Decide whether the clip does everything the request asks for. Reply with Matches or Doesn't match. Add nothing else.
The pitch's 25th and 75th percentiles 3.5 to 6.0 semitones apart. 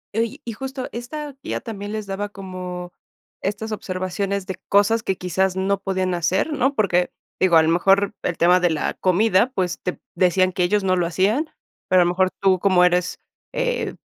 Doesn't match